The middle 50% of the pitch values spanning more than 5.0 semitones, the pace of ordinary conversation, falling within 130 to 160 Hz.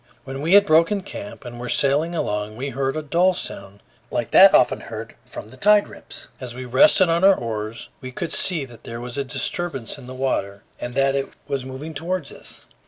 No: wide, 5.4 semitones; fast, 215 wpm; low, 135 Hz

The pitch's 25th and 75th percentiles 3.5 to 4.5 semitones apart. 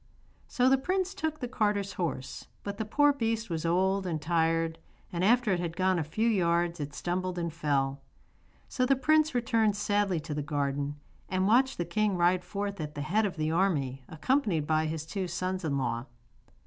No: average, 5.3 semitones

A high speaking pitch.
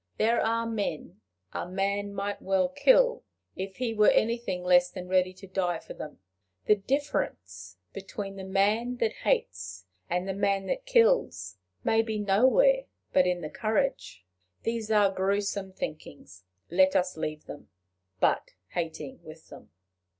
Yes: high, 195 Hz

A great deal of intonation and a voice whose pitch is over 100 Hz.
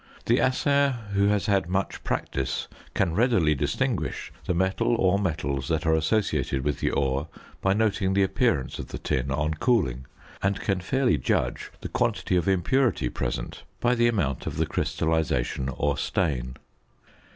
No: wide, 6.8 semitones; very low, 90 Hz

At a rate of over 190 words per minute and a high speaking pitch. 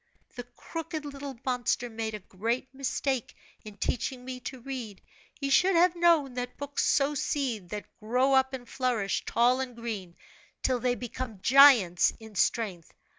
No: average, 160 wpm; very high, 250 Hz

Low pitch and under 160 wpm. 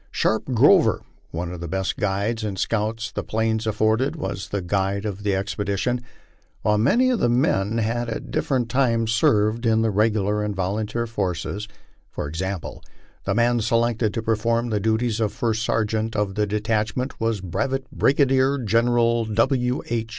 No: low, 110 Hz; average, 165 wpm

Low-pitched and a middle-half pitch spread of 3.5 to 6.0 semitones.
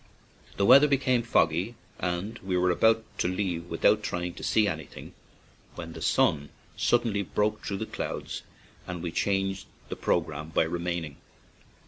Yes: very low, 90 Hz; average, 3.9 semitones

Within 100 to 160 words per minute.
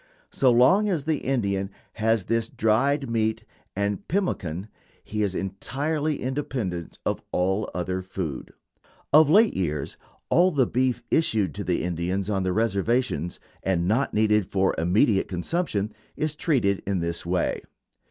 Yes: average, 140 wpm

